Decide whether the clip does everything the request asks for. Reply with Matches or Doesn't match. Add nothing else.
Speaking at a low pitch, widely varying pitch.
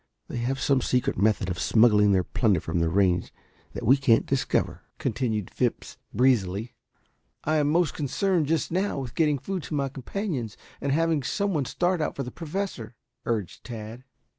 Matches